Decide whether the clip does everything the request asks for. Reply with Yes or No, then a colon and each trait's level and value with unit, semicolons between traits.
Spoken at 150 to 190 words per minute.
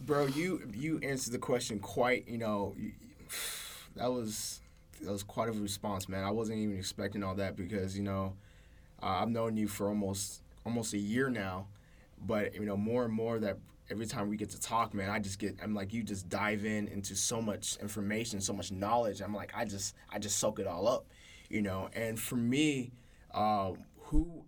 No: fast, 205 wpm